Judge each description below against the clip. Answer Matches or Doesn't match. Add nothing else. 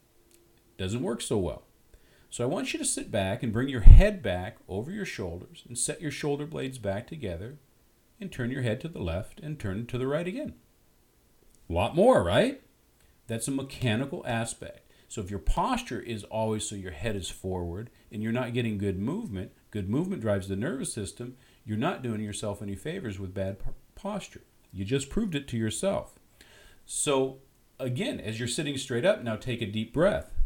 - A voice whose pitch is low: Matches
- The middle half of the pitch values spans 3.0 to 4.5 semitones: Matches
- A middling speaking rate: Matches